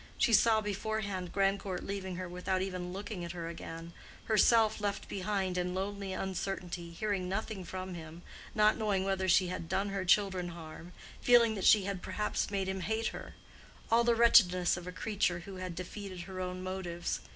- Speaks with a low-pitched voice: No, high, 190 Hz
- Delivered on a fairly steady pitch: Yes, narrow, 2.2 semitones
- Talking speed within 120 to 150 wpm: No, average, 160 wpm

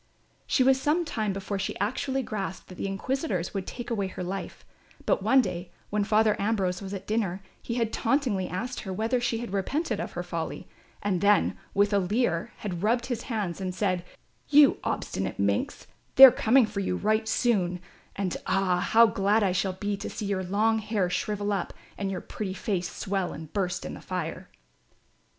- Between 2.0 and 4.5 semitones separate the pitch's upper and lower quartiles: Yes, average, 3.3 semitones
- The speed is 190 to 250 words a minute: Yes, average, 195 wpm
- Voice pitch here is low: No, high, 205 Hz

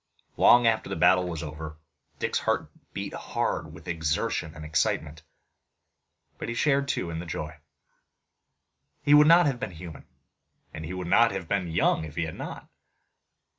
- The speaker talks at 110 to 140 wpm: No, average, 170 wpm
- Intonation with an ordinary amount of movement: No, wide, 6.4 semitones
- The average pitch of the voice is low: Yes, very low, 85 Hz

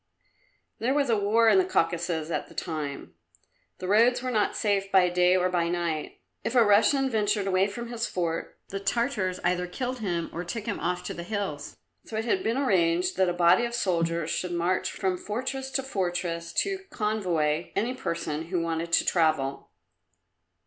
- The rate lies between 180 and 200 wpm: Yes, average, 185 wpm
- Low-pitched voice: No, medium, 185 Hz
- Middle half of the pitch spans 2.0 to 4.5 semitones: No, average, 5.0 semitones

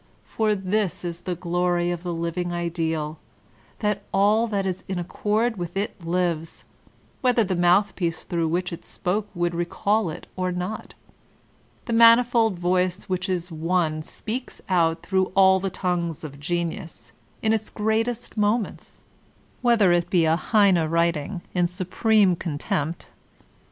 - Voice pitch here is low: No, medium, 180 Hz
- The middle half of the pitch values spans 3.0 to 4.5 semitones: Yes, average, 3.4 semitones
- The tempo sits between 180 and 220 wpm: No, average, 145 wpm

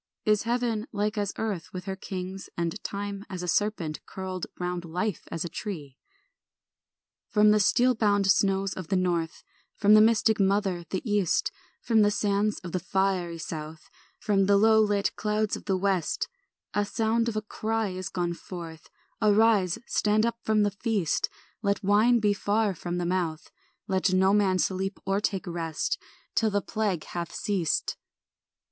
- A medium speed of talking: Yes, average, 170 wpm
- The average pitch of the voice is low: No, high, 200 Hz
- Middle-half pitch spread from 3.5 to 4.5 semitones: No, average, 2.8 semitones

